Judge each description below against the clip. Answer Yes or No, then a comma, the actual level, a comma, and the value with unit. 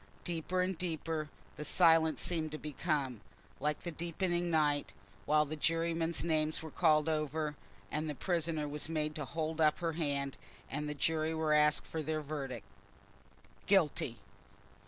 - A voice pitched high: No, medium, 155 Hz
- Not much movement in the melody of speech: Yes, narrow, 1.5 semitones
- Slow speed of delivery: No, average, 155 wpm